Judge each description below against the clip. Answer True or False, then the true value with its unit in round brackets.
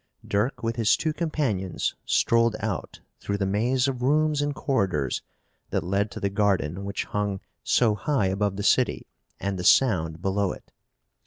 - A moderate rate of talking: True (165 wpm)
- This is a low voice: True (105 Hz)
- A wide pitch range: False (4.4 semitones)